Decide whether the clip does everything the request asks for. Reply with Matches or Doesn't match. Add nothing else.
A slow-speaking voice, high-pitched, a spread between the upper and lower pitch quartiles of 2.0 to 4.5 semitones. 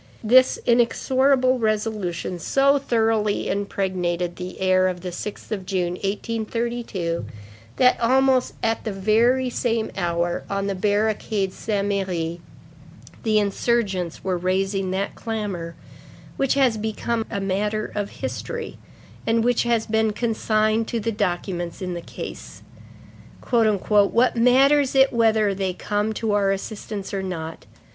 Matches